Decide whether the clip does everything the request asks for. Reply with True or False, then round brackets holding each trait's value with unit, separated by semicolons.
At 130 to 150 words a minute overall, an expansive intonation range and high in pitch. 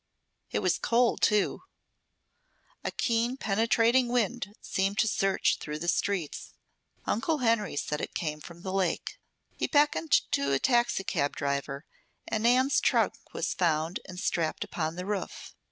True (145 wpm; 6.4 semitones; 195 Hz)